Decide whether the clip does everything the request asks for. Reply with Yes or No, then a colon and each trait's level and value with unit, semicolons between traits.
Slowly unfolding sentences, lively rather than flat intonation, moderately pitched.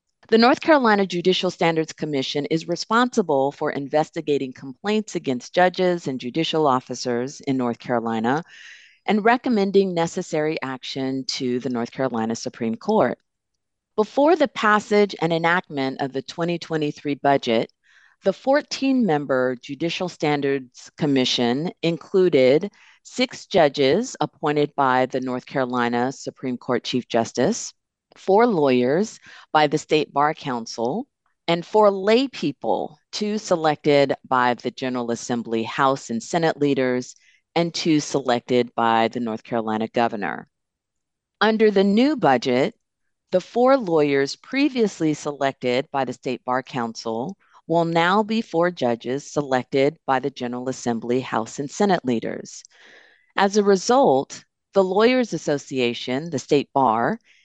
Yes: slow, 125 wpm; wide, 6.5 semitones; medium, 145 Hz